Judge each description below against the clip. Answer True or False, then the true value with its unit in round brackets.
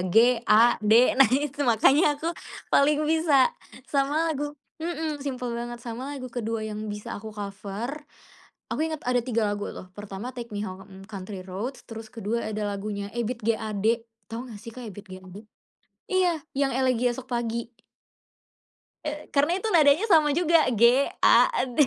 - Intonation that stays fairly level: False (5.0 semitones)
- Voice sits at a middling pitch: False (240 Hz)